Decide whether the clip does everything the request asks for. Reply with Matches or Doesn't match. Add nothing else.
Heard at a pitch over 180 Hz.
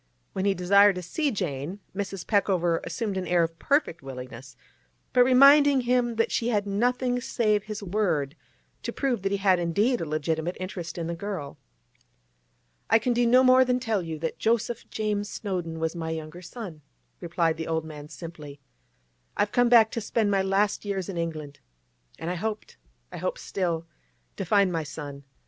Matches